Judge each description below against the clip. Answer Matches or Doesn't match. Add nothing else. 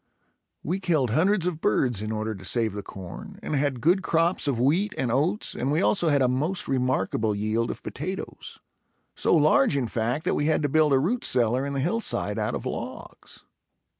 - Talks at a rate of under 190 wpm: Doesn't match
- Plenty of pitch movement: Matches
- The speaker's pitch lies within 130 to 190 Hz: Matches